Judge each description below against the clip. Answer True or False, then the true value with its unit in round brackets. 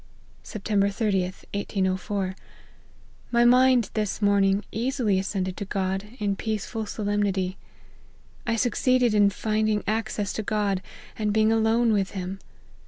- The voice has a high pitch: True (210 Hz)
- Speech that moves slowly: True (125 wpm)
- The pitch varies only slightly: True (2.2 semitones)